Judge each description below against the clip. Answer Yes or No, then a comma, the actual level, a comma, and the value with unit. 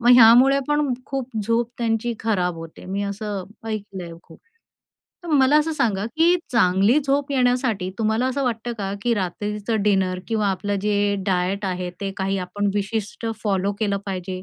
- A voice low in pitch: No, high, 210 Hz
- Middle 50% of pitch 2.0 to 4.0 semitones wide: Yes, average, 3.7 semitones